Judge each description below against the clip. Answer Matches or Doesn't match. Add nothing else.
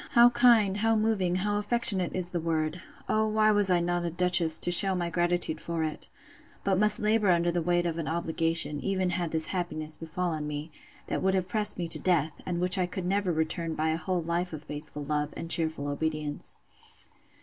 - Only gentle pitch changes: Doesn't match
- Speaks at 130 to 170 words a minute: Doesn't match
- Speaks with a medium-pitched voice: Matches